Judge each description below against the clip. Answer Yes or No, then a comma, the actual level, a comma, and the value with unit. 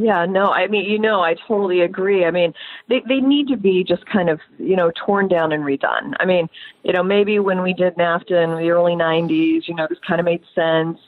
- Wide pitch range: No, average, 3.0 semitones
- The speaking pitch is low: No, medium, 175 Hz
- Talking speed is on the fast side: Yes, fast, 250 wpm